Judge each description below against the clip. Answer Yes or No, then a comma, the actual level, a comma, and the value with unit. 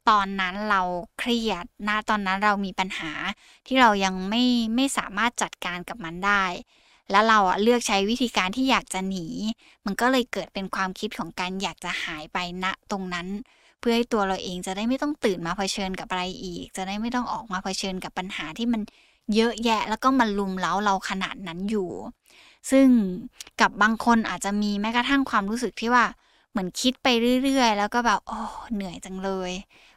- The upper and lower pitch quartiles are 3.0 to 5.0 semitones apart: Yes, average, 3.9 semitones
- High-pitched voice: Yes, high, 205 Hz